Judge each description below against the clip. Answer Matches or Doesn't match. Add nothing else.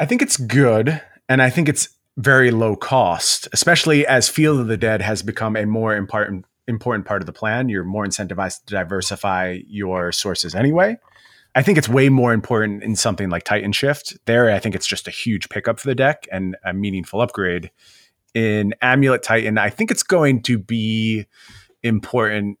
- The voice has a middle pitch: Doesn't match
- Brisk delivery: Doesn't match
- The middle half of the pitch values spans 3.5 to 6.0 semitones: Matches